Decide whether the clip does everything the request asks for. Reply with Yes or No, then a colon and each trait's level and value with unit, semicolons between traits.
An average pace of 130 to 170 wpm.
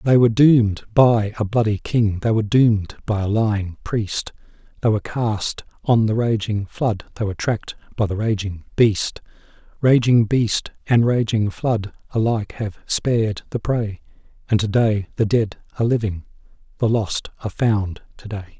Yes: average, 165 wpm